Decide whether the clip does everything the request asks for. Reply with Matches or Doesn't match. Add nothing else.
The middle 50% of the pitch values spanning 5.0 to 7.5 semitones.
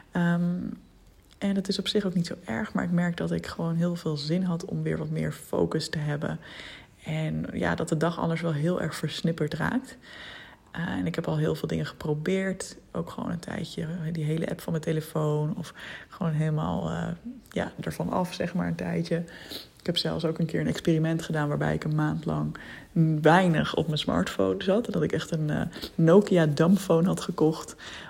Doesn't match